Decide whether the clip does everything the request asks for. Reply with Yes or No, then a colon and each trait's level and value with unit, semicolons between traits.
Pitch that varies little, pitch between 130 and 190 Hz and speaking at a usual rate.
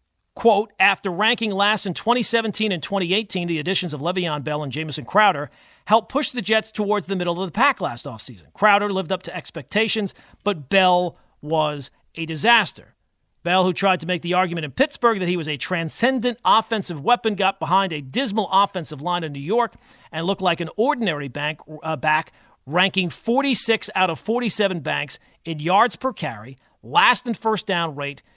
No: wide, 5.4 semitones; medium, 185 Hz; average, 180 wpm